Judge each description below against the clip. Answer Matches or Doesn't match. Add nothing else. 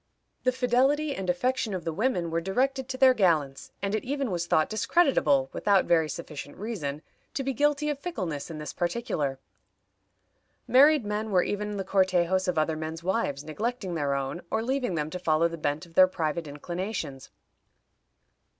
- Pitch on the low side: Doesn't match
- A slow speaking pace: Doesn't match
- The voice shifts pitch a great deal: Matches